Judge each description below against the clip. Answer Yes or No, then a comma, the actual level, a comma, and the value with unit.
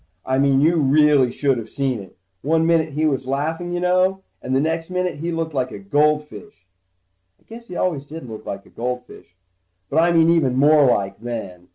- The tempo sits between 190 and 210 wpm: Yes, fast, 205 wpm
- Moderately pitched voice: Yes, medium, 150 Hz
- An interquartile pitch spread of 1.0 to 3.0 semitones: No, average, 4.3 semitones